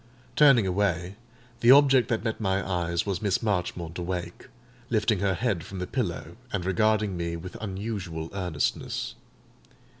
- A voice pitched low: Yes, very low, 95 Hz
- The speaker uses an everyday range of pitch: Yes, average, 3.6 semitones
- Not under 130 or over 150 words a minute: Yes, average, 145 wpm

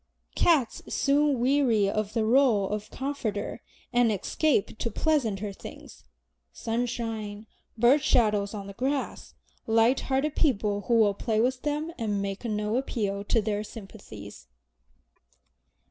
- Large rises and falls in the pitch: No, average, 4.1 semitones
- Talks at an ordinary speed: No, slow, 130 wpm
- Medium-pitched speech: No, high, 225 Hz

